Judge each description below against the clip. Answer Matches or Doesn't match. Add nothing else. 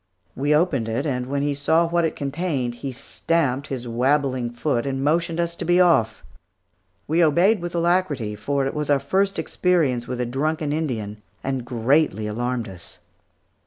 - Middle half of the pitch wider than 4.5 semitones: Matches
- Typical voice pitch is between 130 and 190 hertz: Matches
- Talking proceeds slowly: Doesn't match